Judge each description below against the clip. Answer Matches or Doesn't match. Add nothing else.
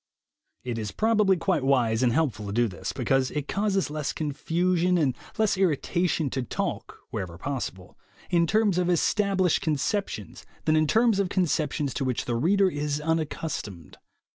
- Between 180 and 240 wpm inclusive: Doesn't match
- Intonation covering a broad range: Matches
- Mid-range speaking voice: Matches